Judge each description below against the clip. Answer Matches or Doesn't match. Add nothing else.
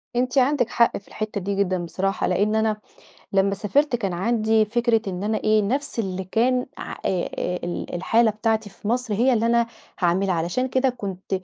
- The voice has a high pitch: Matches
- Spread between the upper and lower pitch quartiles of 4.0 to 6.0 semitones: Doesn't match